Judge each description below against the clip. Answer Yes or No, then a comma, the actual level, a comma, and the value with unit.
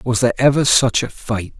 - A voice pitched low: Yes, low, 120 Hz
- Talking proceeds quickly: Yes, fast, 225 wpm